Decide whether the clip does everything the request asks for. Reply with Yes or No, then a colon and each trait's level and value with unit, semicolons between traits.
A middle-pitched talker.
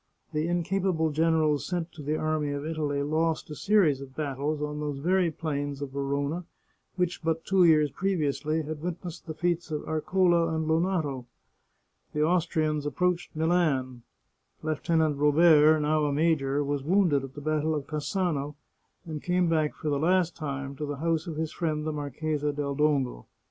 Yes: medium, 155 Hz